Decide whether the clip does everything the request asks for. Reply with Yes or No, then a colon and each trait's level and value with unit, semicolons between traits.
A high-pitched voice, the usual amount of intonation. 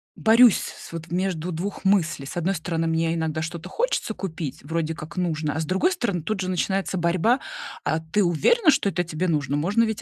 No: medium, 175 Hz; average, 3.6 semitones